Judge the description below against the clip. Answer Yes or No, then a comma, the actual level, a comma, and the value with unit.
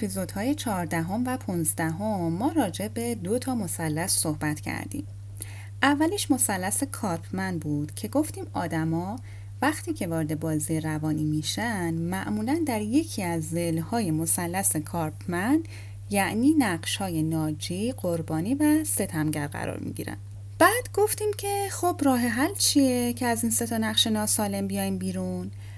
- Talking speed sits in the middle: Yes, average, 135 wpm